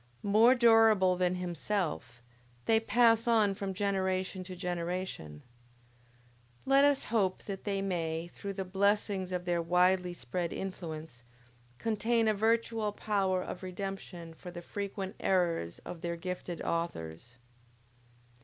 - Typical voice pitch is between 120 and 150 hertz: No, medium, 185 Hz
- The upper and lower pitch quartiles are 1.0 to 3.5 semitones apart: Yes, average, 3.0 semitones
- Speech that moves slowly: Yes, slow, 125 wpm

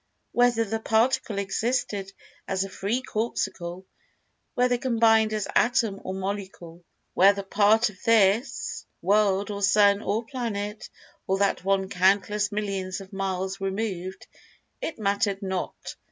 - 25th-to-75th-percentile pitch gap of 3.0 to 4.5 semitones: No, narrow, 2.4 semitones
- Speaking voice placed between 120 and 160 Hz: No, high, 200 Hz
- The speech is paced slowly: Yes, slow, 115 wpm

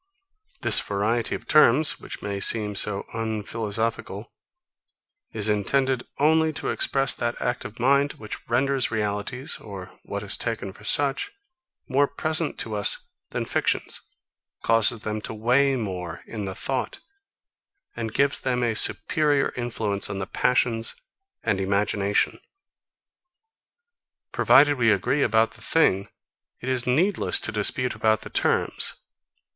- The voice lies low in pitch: Yes, low, 115 Hz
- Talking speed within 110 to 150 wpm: Yes, slow, 135 wpm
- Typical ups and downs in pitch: Yes, average, 4.4 semitones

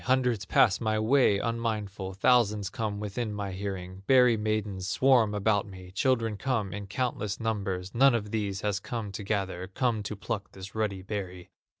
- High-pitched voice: No, low, 105 Hz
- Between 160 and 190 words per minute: Yes, average, 170 wpm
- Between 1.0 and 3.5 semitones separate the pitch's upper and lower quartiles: Yes, average, 2.8 semitones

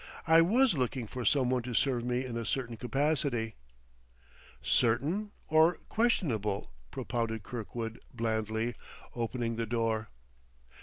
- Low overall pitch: Yes, low, 120 Hz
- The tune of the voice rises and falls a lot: No, average, 3.6 semitones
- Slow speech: Yes, slow, 130 wpm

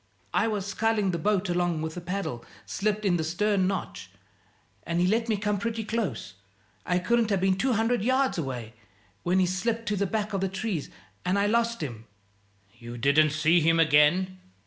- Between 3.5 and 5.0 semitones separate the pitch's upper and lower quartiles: Yes, average, 4.5 semitones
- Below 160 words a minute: No, average, 190 wpm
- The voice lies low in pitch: No, high, 190 Hz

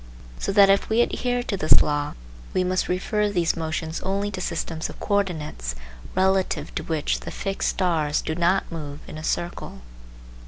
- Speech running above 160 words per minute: Yes, average, 170 wpm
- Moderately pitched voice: Yes, medium, 180 Hz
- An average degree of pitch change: Yes, average, 3.7 semitones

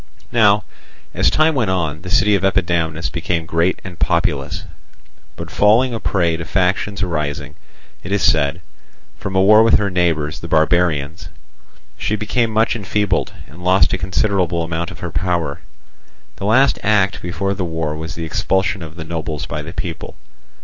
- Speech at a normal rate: Yes, average, 170 wpm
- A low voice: Yes, very low, 90 Hz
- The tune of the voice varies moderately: Yes, average, 3.5 semitones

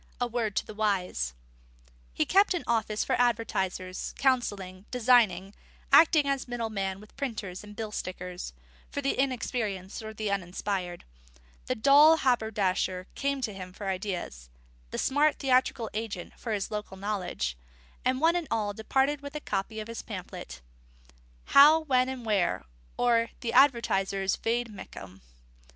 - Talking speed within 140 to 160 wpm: Yes, average, 145 wpm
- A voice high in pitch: Yes, high, 220 Hz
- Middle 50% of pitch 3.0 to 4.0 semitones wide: No, average, 4.9 semitones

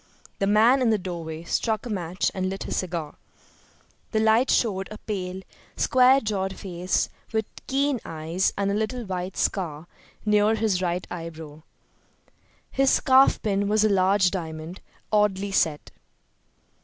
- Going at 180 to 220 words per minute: No, average, 145 wpm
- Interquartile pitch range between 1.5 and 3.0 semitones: No, average, 3.5 semitones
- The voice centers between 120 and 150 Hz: No, high, 195 Hz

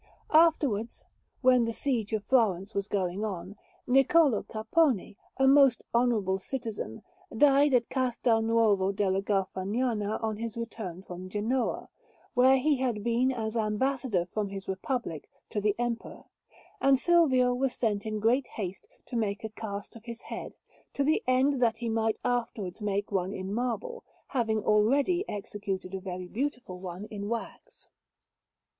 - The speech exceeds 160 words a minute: No, average, 150 wpm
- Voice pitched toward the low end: No, high, 225 Hz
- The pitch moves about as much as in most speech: Yes, average, 4.1 semitones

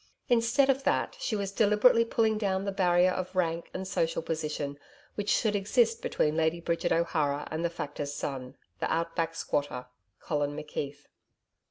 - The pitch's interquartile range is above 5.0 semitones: Yes, wide, 5.4 semitones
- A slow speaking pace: No, average, 165 wpm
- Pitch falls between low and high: Yes, medium, 170 Hz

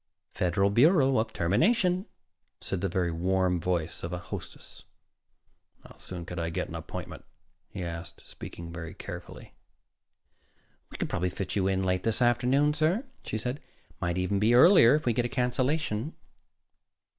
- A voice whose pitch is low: Yes, low, 100 Hz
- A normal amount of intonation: No, wide, 6.5 semitones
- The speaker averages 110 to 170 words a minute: Yes, average, 160 wpm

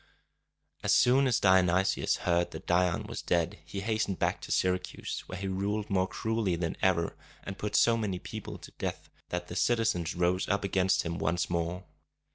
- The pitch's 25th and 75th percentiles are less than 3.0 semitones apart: Yes, narrow, 2.5 semitones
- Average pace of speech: Yes, average, 180 wpm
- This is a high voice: No, very low, 95 Hz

